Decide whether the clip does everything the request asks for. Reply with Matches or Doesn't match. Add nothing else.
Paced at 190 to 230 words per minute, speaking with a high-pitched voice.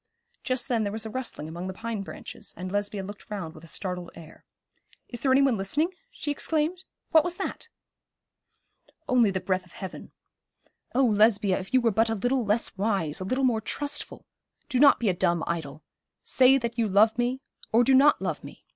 Matches